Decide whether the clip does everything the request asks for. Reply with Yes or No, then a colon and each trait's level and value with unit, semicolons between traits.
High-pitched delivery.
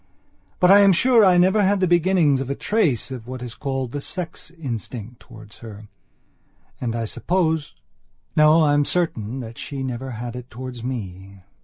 No: low, 130 Hz